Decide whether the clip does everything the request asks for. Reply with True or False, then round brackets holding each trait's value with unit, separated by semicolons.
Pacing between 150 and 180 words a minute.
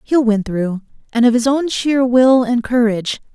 False (200 wpm)